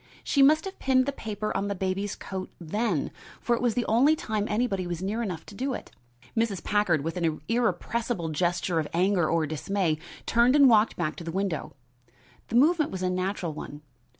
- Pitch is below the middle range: No, high, 200 Hz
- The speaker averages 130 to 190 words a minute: No, average, 200 wpm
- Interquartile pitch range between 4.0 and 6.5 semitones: Yes, average, 5.3 semitones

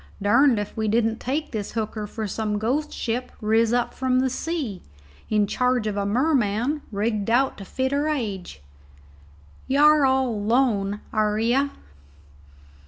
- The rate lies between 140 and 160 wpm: Yes, average, 150 wpm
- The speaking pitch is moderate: No, high, 230 Hz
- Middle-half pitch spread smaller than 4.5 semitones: Yes, average, 3.9 semitones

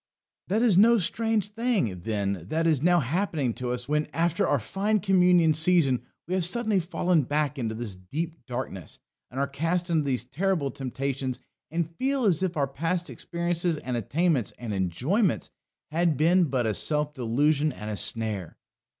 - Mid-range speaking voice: Yes, medium, 155 Hz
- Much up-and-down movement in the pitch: Yes, wide, 6.2 semitones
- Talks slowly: No, average, 175 wpm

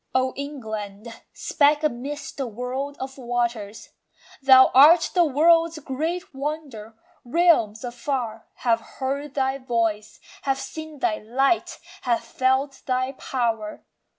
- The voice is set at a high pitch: Yes, very high, 260 Hz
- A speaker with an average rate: No, slow, 120 wpm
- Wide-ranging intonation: No, average, 3.6 semitones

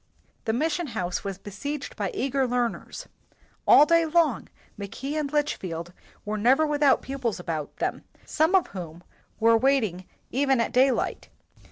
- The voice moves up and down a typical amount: No, wide, 6.4 semitones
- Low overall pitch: No, very high, 255 Hz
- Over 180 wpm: No, average, 155 wpm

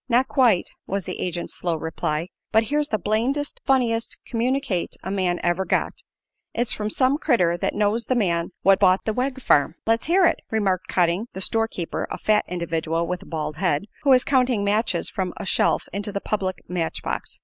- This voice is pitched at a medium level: No, high, 200 Hz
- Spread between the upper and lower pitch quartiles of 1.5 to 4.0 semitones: No, average, 5.2 semitones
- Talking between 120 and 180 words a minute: No, average, 195 wpm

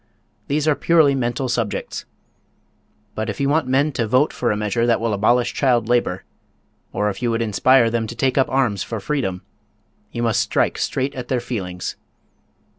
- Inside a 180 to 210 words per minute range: Yes, average, 185 wpm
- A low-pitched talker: Yes, low, 120 Hz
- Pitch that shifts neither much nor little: Yes, average, 3.3 semitones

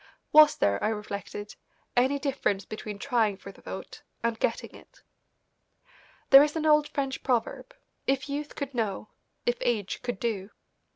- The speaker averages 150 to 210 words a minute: Yes, average, 155 wpm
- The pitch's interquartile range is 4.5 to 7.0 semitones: Yes, average, 5.2 semitones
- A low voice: No, high, 245 Hz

